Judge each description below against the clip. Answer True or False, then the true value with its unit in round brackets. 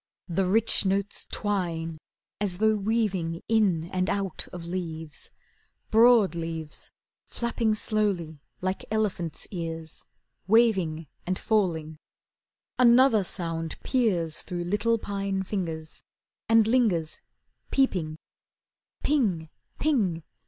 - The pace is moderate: False (95 wpm)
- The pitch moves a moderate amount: True (4.8 semitones)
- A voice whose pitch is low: False (190 Hz)